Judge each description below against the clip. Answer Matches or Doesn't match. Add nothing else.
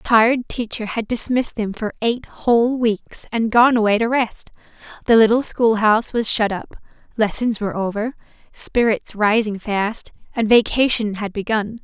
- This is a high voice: Matches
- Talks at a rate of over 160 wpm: Doesn't match